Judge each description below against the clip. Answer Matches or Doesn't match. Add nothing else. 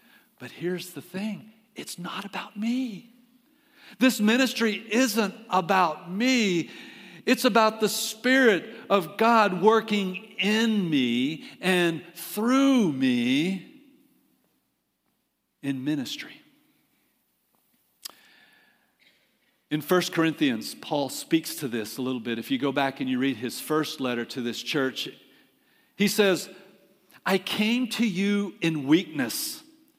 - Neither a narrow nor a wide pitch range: Doesn't match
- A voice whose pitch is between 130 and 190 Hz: Doesn't match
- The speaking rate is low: Matches